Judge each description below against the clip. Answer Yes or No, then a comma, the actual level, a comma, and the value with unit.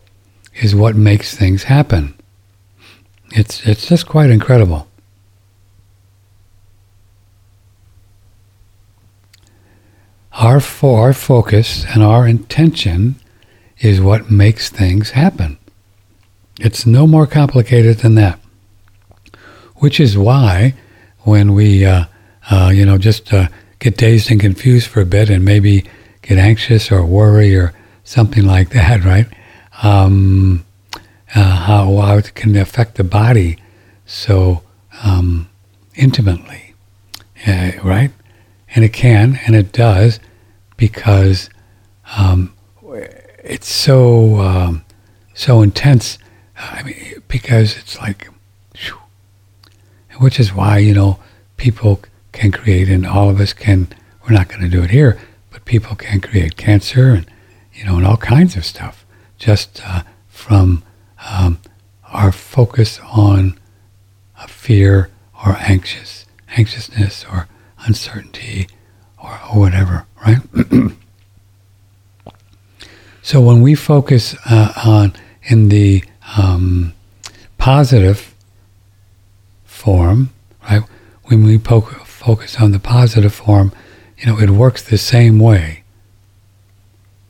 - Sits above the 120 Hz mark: No, low, 100 Hz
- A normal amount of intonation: No, narrow, 2.1 semitones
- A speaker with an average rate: No, slow, 115 wpm